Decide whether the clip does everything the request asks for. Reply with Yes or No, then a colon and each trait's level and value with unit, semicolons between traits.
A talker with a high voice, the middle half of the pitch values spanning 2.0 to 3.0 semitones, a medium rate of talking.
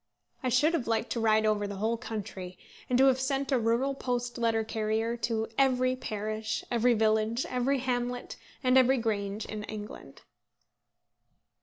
Yes: high, 230 Hz; average, 2.7 semitones; average, 160 wpm